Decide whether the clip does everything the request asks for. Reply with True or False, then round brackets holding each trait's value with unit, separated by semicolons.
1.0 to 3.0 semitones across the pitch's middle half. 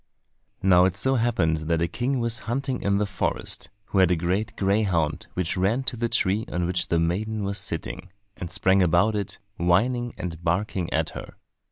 False (4.1 semitones)